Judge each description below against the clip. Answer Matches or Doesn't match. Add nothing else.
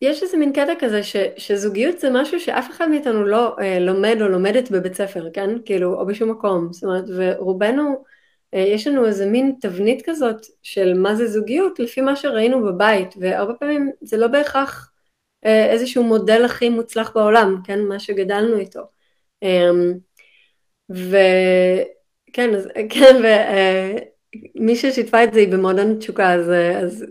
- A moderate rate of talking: Doesn't match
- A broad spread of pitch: Doesn't match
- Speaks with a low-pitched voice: Doesn't match